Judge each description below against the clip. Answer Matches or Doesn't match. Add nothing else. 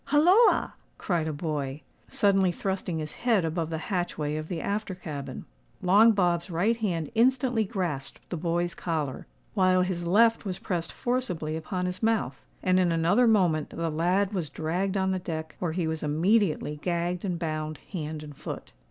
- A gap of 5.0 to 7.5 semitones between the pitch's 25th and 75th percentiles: Doesn't match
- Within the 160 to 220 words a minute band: Matches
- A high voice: Doesn't match